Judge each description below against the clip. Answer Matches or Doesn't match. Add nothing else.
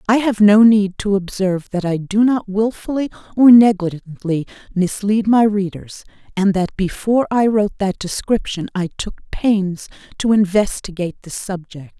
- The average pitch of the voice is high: Matches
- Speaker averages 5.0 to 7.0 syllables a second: Doesn't match